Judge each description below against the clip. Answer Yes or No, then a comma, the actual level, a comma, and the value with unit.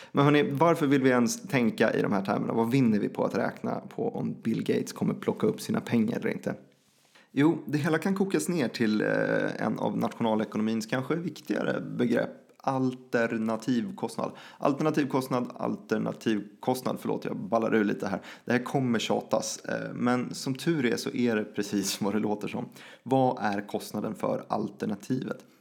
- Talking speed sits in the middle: Yes, average, 165 wpm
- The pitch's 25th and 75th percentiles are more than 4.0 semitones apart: Yes, average, 4.6 semitones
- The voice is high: No, low, 125 Hz